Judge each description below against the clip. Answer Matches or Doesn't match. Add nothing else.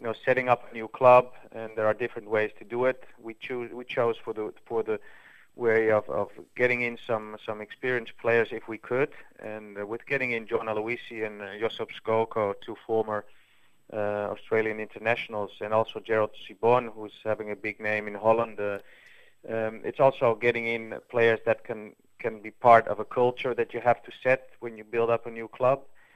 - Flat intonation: Matches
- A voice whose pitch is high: Doesn't match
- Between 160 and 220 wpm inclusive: Matches